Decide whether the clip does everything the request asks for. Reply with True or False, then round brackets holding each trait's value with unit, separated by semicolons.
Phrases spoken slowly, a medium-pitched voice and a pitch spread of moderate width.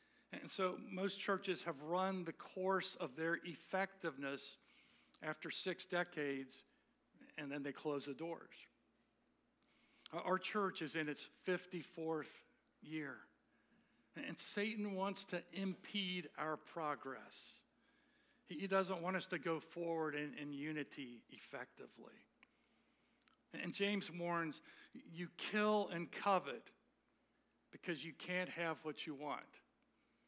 True (115 wpm; 170 Hz; 3.5 semitones)